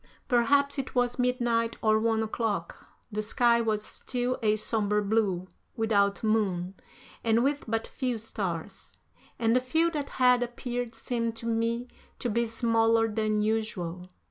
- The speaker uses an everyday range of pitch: No, narrow, 2.3 semitones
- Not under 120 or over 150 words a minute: Yes, average, 145 wpm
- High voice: Yes, high, 225 Hz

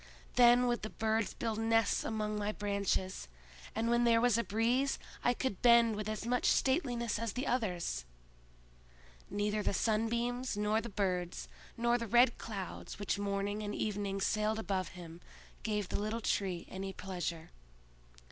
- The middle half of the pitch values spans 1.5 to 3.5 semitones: Yes, average, 2.8 semitones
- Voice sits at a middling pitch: No, high, 215 Hz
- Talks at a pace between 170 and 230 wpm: No, average, 155 wpm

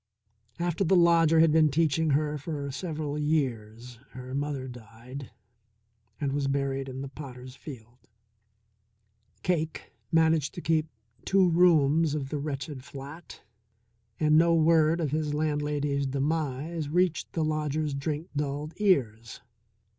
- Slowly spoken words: Yes, slow, 130 wpm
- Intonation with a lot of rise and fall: No, average, 2.8 semitones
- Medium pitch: Yes, medium, 150 Hz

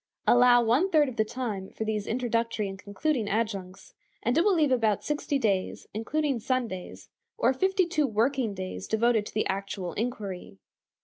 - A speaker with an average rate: Yes, average, 170 wpm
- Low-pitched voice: No, high, 230 Hz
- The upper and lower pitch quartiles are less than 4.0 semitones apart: No, average, 4.4 semitones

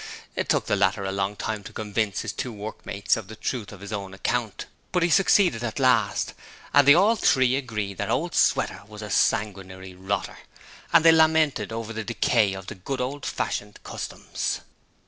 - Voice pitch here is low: Yes, low, 110 Hz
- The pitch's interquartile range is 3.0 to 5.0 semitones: Yes, average, 4.6 semitones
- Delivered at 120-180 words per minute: No, average, 190 wpm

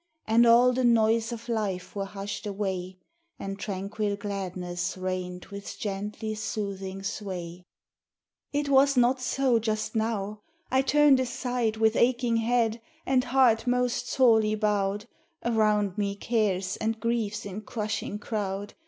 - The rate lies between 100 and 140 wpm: Yes, slow, 135 wpm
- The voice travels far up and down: No, average, 3.1 semitones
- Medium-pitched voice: No, high, 215 Hz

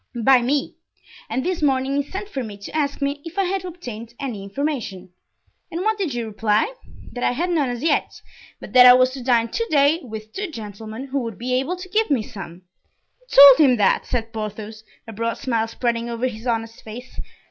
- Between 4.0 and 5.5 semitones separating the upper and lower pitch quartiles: Yes, average, 4.6 semitones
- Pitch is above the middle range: Yes, very high, 250 Hz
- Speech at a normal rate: No, fast, 215 wpm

